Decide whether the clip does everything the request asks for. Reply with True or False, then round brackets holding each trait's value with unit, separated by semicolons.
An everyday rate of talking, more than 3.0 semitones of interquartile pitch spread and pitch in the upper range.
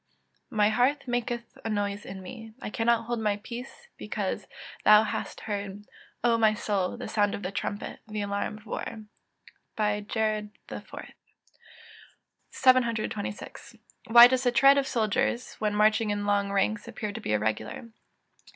False (150 wpm; 2.5 semitones; 215 Hz)